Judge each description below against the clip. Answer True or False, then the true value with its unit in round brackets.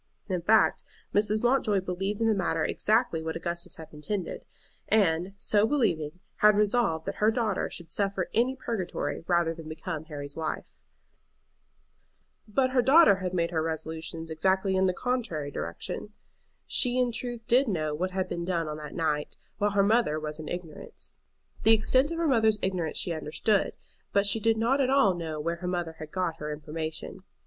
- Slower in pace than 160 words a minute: False (175 wpm)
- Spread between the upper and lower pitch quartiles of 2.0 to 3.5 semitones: False (5.4 semitones)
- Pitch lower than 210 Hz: True (185 Hz)